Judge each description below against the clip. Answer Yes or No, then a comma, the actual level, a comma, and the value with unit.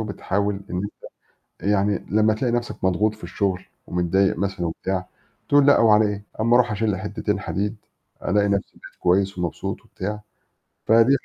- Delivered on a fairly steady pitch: Yes, narrow, 2.3 semitones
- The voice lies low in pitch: Yes, low, 100 Hz